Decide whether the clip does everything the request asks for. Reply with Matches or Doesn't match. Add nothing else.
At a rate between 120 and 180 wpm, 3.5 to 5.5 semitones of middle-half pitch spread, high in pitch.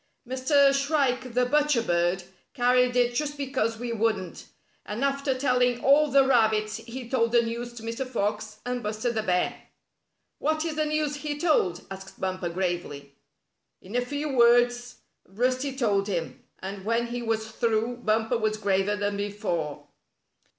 Matches